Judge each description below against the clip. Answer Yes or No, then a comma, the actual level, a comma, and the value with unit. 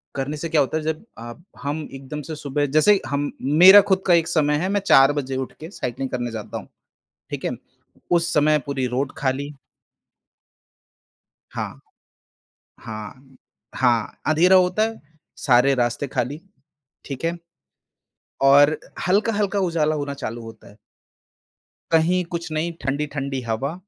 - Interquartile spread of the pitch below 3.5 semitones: No, average, 3.9 semitones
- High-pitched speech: No, medium, 145 Hz